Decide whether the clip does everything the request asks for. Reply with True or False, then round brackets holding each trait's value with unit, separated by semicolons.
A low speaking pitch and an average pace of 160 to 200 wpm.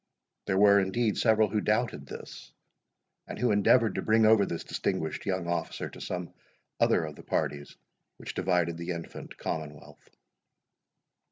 False (95 Hz; 150 wpm)